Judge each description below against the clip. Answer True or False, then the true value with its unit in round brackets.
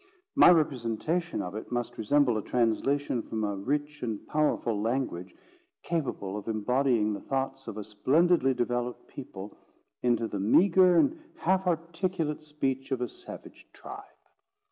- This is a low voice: True (130 Hz)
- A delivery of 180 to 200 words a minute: False (145 wpm)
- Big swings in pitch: True (5.7 semitones)